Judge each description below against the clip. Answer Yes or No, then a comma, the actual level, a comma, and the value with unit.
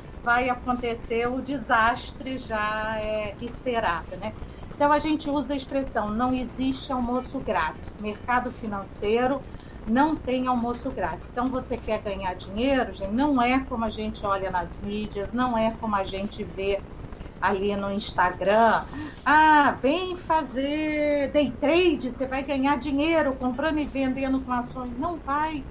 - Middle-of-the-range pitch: No, very high, 250 Hz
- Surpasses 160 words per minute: No, average, 145 wpm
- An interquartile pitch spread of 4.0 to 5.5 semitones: Yes, average, 4.4 semitones